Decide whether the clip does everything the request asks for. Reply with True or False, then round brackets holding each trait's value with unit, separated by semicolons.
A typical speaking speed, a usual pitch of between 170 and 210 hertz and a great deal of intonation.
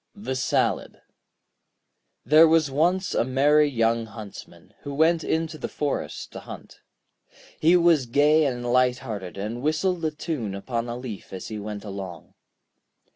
False (155 wpm; 130 Hz; 5.7 semitones)